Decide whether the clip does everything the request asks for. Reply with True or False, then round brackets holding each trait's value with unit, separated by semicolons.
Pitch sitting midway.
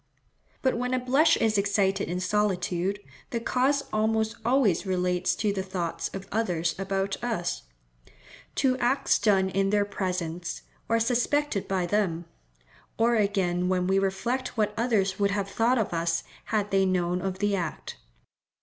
False (195 Hz)